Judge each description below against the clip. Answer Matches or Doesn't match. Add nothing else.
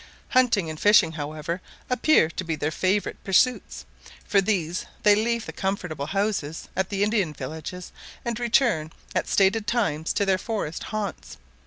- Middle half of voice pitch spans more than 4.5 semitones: Matches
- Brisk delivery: Doesn't match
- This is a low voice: Doesn't match